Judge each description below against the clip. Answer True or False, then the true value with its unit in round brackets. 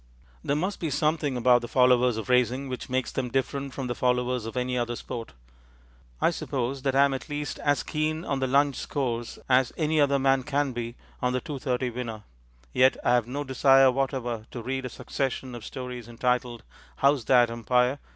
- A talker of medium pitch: False (130 Hz)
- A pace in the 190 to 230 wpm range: True (200 wpm)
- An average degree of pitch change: False (2.1 semitones)